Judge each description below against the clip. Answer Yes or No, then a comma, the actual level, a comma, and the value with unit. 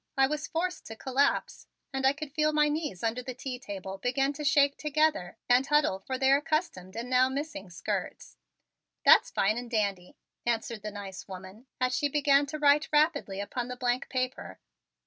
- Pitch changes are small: No, average, 4.8 semitones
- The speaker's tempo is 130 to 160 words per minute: No, average, 185 wpm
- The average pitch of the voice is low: No, very high, 260 Hz